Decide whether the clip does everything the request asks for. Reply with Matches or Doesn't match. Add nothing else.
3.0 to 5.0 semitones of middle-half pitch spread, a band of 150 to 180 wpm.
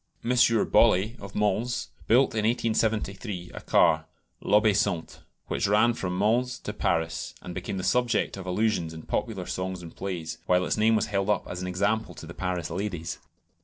Matches